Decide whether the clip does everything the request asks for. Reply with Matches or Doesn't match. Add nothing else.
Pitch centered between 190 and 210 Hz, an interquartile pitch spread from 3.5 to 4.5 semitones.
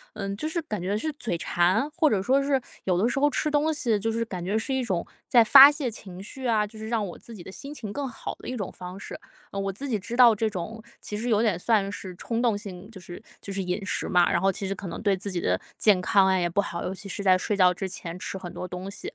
Matches